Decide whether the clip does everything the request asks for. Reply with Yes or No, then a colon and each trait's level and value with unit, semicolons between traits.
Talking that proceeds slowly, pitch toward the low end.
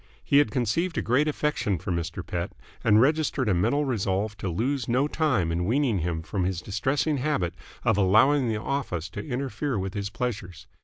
No: average, 190 wpm; low, 110 Hz